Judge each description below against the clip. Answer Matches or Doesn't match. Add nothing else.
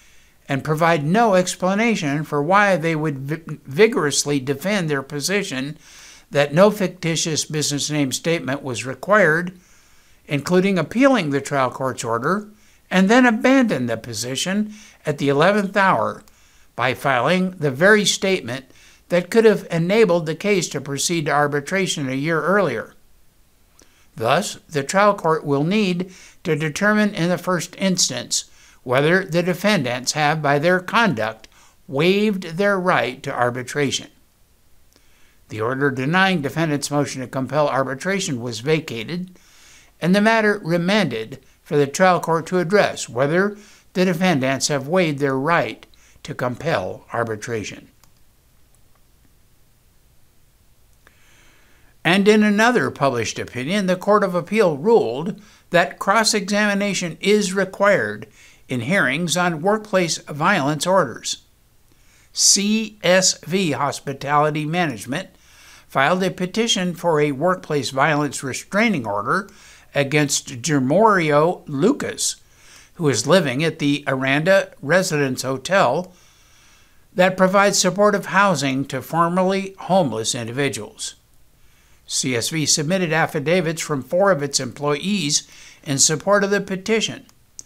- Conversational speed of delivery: Doesn't match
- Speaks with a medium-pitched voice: Matches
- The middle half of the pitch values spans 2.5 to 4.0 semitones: Doesn't match